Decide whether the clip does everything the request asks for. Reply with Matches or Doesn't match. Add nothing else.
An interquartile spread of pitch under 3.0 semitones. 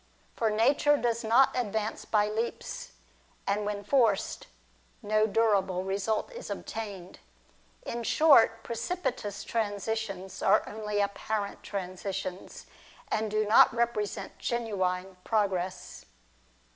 Matches